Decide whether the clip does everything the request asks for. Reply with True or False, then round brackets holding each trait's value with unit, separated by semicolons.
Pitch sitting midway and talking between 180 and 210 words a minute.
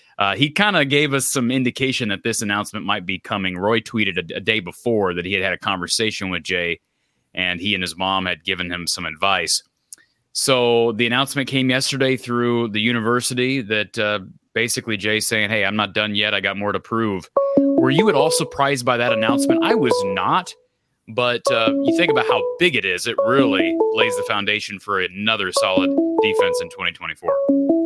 False (120 Hz; 200 wpm)